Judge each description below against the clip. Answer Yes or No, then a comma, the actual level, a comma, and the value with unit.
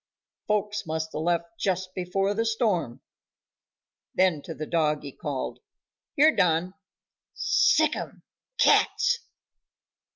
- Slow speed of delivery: Yes, slow, 100 wpm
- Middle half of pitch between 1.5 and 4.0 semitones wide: No, average, 4.7 semitones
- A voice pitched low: No, medium, 180 Hz